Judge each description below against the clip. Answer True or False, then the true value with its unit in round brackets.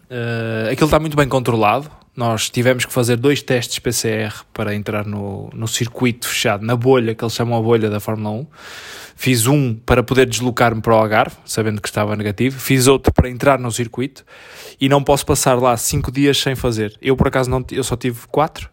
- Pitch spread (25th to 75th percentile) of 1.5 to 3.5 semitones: True (2.9 semitones)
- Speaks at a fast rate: True (205 wpm)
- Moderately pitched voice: False (125 Hz)